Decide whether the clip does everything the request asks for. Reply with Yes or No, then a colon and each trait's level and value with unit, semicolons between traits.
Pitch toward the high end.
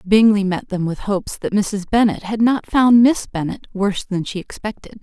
Yes: high, 205 Hz